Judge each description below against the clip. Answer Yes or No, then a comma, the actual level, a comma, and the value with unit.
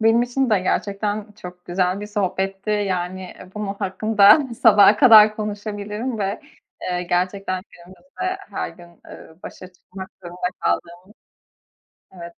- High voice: Yes, high, 200 Hz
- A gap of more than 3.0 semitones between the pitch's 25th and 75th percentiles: No, average, 2.7 semitones